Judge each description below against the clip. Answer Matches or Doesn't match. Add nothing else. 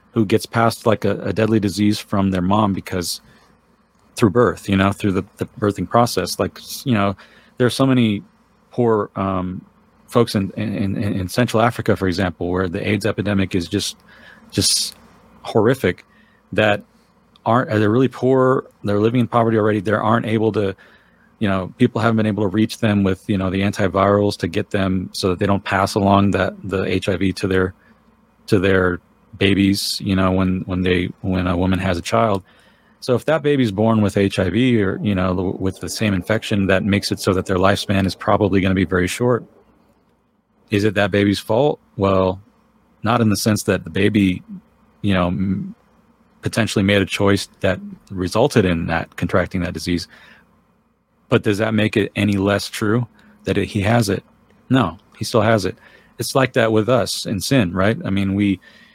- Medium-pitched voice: Doesn't match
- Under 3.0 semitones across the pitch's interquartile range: Matches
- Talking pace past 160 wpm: Matches